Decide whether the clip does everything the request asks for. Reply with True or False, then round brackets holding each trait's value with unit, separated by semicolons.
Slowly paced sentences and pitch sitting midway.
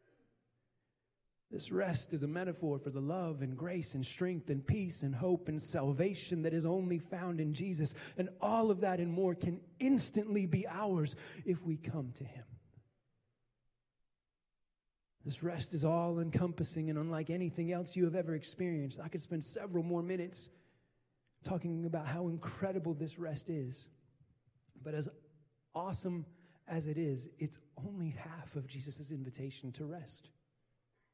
False (150 wpm; 160 Hz)